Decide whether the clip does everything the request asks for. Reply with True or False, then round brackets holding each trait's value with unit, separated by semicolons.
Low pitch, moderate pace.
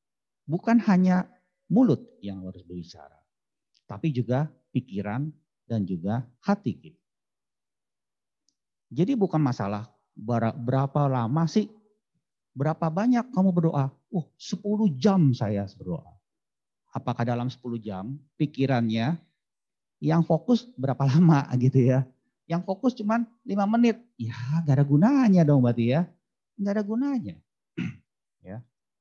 False (145 Hz; 110 wpm)